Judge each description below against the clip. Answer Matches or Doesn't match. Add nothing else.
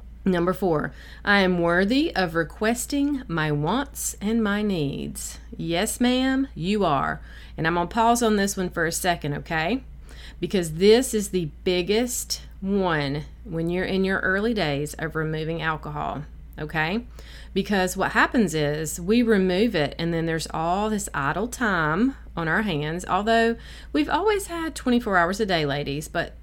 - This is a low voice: Doesn't match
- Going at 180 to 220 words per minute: Doesn't match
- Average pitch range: Doesn't match